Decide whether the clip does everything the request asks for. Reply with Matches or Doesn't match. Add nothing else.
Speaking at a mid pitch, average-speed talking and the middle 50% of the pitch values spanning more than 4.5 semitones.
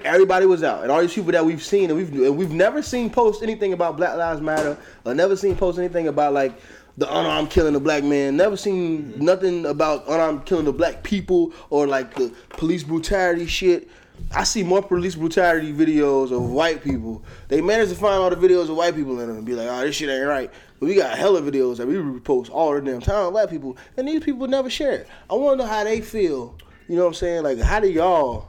Doesn't match